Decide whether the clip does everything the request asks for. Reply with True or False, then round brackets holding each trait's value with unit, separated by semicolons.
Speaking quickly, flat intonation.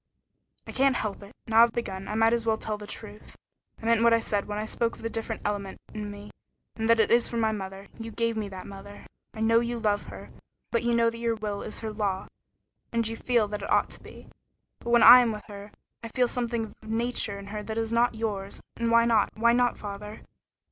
True (250 wpm; 1.9 semitones)